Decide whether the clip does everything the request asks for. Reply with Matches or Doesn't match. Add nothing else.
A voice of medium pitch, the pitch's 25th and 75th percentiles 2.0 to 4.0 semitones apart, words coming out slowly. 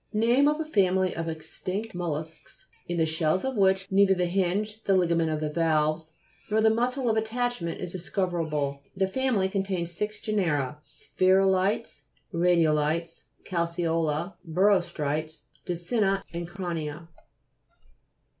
Matches